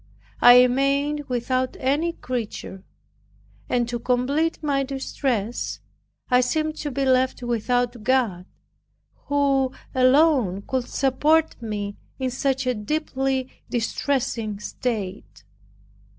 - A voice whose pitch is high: Yes, very high, 255 Hz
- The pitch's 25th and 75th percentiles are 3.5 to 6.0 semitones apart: No, narrow, 2.5 semitones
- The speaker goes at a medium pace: No, slow, 105 wpm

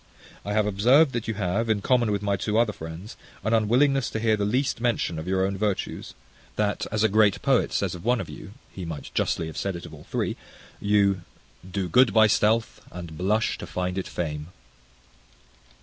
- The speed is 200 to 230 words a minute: Yes, fast, 205 wpm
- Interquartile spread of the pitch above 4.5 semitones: No, average, 3.3 semitones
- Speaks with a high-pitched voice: No, low, 105 Hz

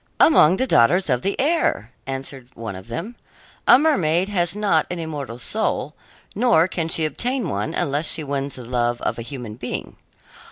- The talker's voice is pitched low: No, medium, 155 Hz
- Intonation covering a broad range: Yes, wide, 7.8 semitones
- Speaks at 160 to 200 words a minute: Yes, average, 175 wpm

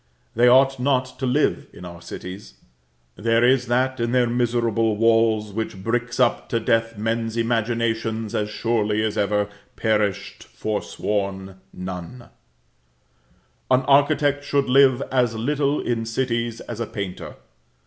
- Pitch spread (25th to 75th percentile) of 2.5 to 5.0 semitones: Yes, average, 2.8 semitones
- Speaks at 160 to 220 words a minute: No, slow, 135 wpm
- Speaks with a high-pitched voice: No, low, 115 Hz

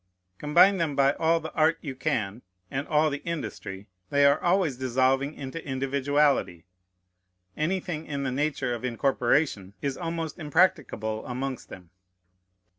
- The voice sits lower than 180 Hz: Yes, medium, 140 Hz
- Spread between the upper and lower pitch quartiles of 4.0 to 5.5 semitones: No, average, 3.4 semitones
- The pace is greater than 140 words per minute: No, slow, 135 wpm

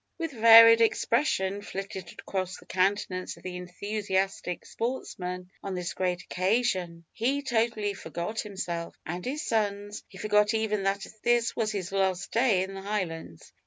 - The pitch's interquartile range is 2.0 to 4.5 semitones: Yes, average, 3.4 semitones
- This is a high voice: Yes, high, 195 Hz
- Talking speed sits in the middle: Yes, average, 150 wpm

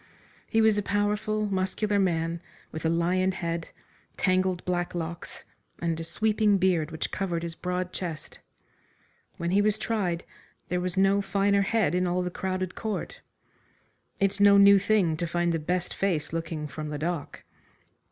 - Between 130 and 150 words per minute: No, average, 160 wpm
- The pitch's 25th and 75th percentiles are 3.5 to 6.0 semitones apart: No, average, 2.9 semitones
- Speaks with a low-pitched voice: No, medium, 180 Hz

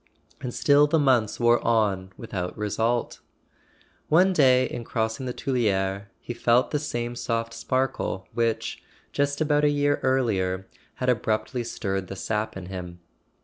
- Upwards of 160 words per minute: No, average, 155 wpm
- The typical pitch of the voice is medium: No, low, 120 Hz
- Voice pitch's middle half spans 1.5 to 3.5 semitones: No, average, 4.2 semitones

